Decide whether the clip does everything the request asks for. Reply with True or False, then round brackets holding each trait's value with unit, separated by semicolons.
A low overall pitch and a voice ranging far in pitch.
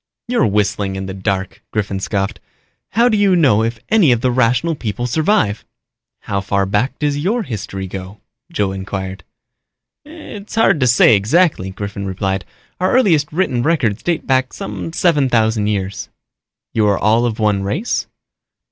True (110 Hz; 8.0 semitones)